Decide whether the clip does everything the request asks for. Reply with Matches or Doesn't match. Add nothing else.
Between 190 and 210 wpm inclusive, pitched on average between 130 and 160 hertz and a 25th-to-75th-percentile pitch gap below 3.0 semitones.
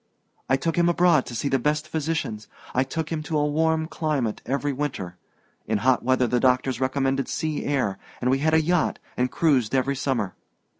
Doesn't match